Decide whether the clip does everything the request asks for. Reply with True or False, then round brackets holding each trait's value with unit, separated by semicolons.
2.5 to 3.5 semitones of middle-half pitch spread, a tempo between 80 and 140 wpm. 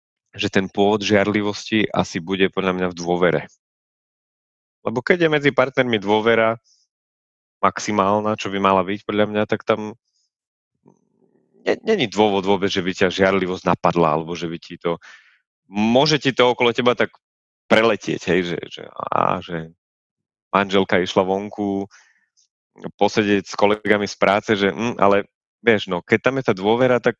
False (2.9 semitones; 155 wpm)